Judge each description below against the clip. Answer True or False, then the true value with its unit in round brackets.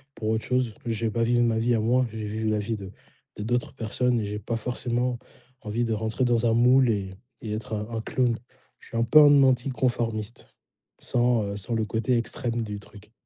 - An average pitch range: False (2.1 semitones)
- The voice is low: True (115 Hz)